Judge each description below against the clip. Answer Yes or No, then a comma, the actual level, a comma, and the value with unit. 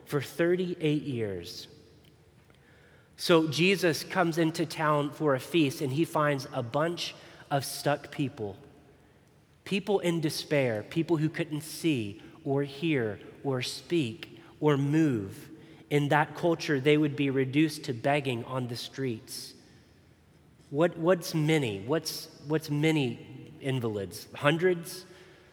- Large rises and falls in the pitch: No, average, 2.8 semitones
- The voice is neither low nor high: Yes, medium, 150 Hz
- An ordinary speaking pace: No, slow, 120 wpm